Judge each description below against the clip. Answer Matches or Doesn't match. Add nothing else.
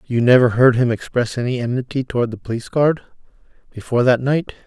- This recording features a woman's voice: Doesn't match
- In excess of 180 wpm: Doesn't match